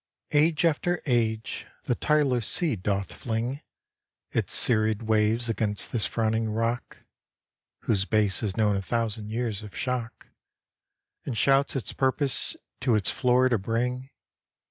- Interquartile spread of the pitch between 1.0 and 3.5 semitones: Yes, average, 2.9 semitones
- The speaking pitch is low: Yes, low, 115 Hz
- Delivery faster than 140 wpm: No, slow, 135 wpm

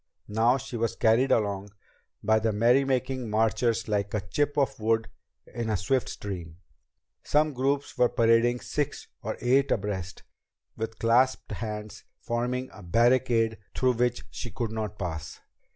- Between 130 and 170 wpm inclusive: Yes, average, 145 wpm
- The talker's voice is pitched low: Yes, low, 115 Hz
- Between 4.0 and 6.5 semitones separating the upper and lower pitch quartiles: No, average, 3.0 semitones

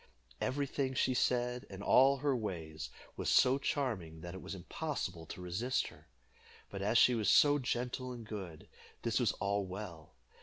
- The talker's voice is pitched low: Yes, low, 115 Hz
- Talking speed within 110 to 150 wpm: No, average, 175 wpm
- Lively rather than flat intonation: Yes, wide, 5.8 semitones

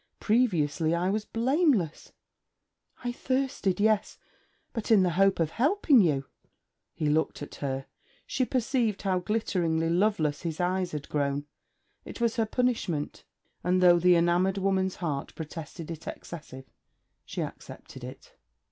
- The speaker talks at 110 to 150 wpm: Yes, average, 140 wpm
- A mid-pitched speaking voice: Yes, medium, 180 Hz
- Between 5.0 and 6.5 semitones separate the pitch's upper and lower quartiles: Yes, average, 5.3 semitones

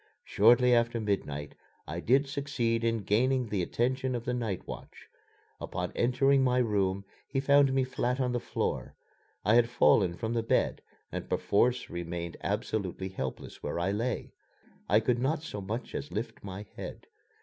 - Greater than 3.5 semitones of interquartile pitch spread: Yes, average, 4.2 semitones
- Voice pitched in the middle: No, low, 115 Hz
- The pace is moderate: Yes, average, 165 wpm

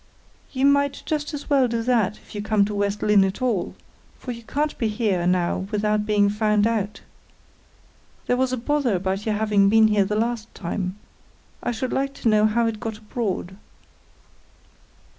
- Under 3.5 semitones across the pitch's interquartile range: Yes, average, 2.9 semitones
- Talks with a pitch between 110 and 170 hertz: No, high, 215 Hz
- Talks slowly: No, average, 180 wpm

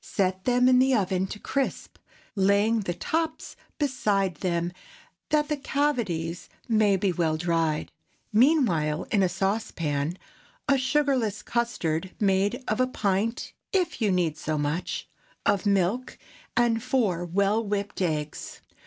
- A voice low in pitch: No, high, 200 Hz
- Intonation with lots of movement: Yes, wide, 5.8 semitones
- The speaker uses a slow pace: Yes, slow, 130 wpm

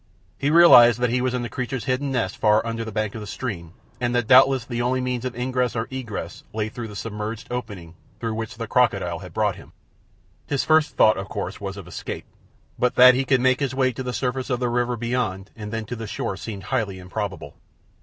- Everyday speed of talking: No, fast, 230 wpm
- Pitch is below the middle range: Yes, low, 120 Hz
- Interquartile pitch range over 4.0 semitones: No, average, 3.1 semitones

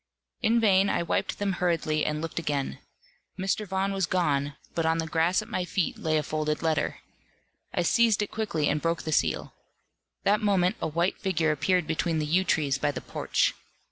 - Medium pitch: Yes, medium, 170 Hz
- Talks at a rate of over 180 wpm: Yes, average, 195 wpm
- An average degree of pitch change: Yes, average, 3.8 semitones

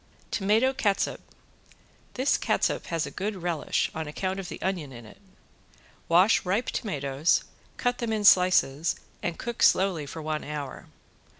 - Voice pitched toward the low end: No, medium, 180 Hz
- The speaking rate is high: No, average, 145 wpm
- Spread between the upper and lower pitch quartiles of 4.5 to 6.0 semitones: Yes, average, 5.1 semitones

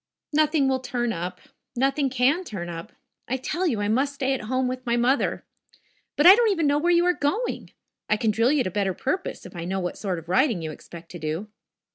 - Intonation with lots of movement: Yes, wide, 7.1 semitones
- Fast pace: Yes, fast, 230 wpm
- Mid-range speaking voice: No, very high, 250 Hz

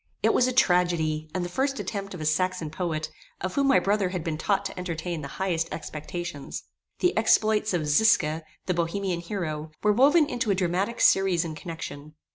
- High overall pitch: No, medium, 180 Hz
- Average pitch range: Yes, average, 4.0 semitones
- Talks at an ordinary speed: Yes, average, 190 wpm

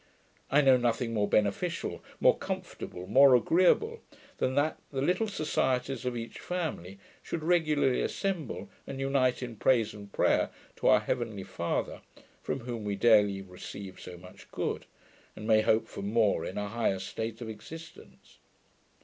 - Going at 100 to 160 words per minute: Yes, average, 155 wpm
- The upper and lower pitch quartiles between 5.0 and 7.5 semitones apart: Yes, wide, 5.5 semitones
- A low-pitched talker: Yes, low, 120 Hz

